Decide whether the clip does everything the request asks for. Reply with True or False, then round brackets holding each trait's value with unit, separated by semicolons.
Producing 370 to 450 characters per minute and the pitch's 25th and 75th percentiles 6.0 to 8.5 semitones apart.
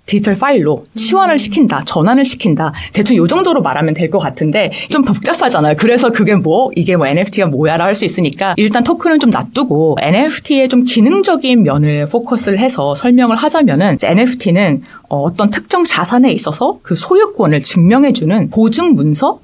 True (375 characters per minute; 6.9 semitones)